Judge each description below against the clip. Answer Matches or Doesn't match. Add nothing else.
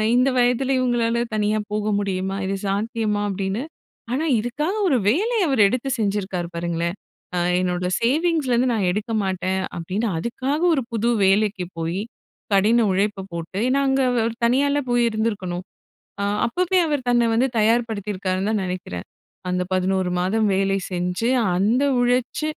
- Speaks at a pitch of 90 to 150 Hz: Doesn't match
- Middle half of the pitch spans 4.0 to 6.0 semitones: Matches